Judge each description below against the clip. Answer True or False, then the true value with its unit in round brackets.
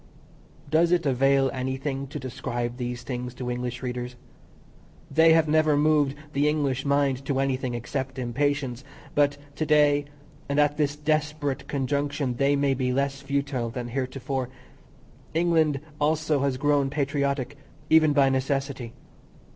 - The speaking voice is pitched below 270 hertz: True (140 Hz)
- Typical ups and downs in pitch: False (2.2 semitones)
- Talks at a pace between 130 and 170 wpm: True (140 wpm)